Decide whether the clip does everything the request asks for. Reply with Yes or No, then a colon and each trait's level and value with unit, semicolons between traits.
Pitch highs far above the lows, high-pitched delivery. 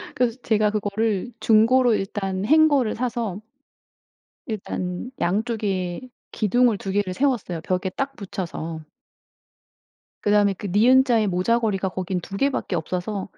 No: average, 4.0 semitones; high, 210 Hz